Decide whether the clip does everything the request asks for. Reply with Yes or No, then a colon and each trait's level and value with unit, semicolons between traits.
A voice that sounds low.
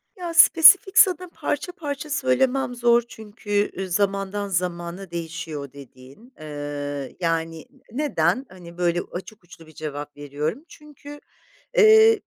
No: high, 195 Hz